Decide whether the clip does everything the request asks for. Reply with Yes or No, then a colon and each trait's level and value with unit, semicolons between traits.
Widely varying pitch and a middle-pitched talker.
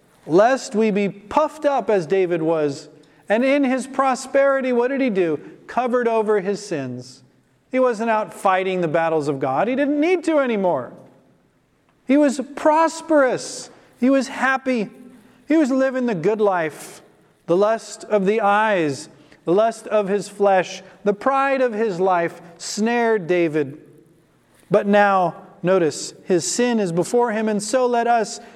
No: wide, 6.1 semitones; high, 215 Hz